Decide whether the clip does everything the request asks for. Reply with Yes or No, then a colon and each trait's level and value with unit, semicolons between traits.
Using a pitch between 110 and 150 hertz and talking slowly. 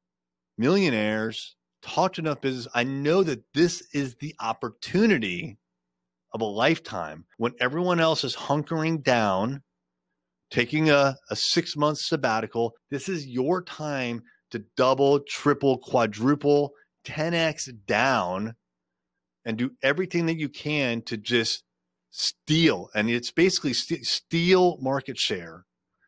Yes: low, 135 Hz; slow, 120 wpm